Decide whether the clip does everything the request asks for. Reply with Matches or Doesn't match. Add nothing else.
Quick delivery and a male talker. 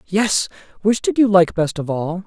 Matches